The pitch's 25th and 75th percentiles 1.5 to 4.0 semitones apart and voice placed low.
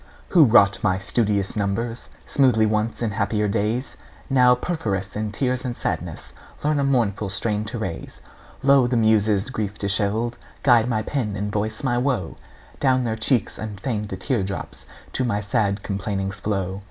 Yes: average, 3.5 semitones; low, 110 Hz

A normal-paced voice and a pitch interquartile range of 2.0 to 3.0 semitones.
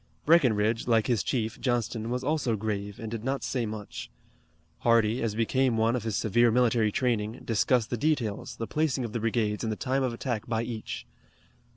Yes: average, 190 wpm; narrow, 2.4 semitones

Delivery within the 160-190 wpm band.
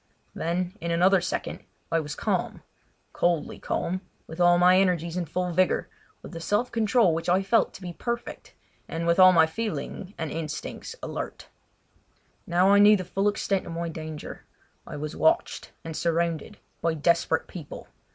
Yes: average, 165 wpm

